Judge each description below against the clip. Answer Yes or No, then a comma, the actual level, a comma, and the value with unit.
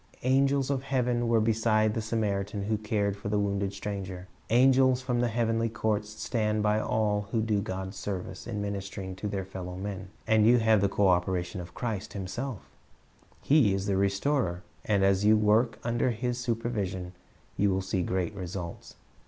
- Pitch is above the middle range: No, low, 105 Hz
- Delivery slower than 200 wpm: Yes, average, 175 wpm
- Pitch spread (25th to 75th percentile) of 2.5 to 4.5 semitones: Yes, average, 3.0 semitones